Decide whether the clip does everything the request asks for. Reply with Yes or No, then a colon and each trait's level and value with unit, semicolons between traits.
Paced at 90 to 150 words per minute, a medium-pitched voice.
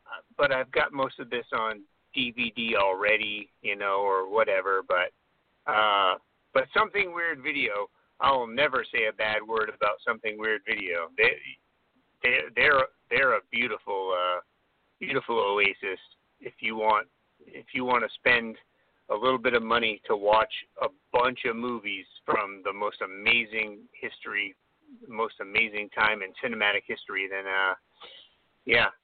No: average, 145 wpm; low, 120 Hz